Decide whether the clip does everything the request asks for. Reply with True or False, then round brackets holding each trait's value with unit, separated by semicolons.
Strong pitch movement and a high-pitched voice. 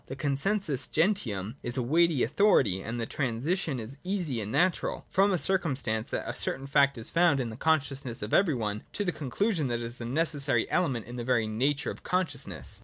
False (6.1 semitones; 135 Hz)